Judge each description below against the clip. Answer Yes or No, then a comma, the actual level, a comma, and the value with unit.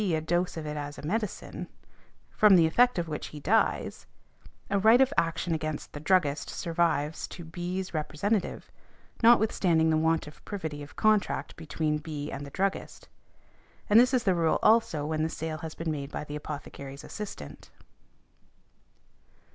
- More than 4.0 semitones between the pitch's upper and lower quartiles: Yes, average, 4.5 semitones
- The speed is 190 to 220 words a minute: No, average, 165 wpm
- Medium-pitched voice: Yes, medium, 160 Hz